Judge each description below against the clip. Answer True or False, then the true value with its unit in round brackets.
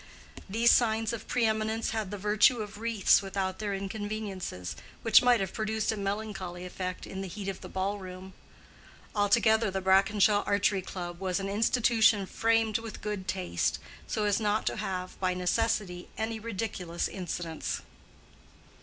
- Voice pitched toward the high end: True (205 Hz)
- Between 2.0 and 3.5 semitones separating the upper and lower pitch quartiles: True (2.7 semitones)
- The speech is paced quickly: False (155 wpm)